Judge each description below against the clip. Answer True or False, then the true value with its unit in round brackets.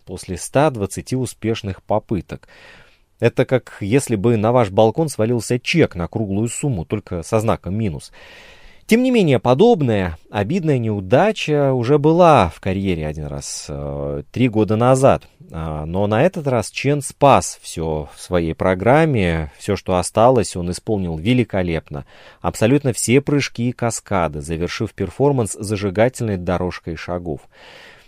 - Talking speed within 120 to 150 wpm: True (130 wpm)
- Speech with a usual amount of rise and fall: False (6.2 semitones)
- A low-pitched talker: True (110 Hz)